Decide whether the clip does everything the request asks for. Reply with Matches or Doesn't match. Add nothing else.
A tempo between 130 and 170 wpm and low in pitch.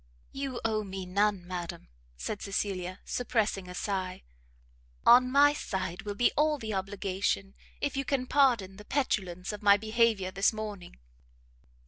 Doesn't match